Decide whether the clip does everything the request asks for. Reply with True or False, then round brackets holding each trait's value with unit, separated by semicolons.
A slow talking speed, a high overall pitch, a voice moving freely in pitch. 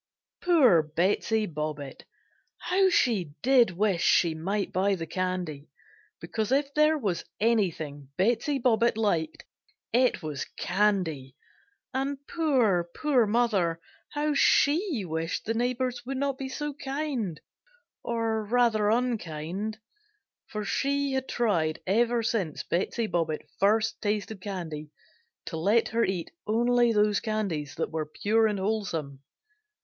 True (125 wpm; 215 Hz; 6.1 semitones)